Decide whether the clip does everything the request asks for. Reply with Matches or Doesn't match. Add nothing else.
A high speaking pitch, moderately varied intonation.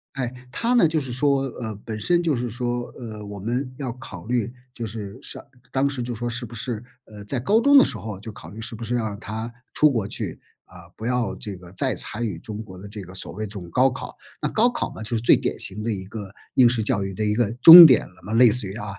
Doesn't match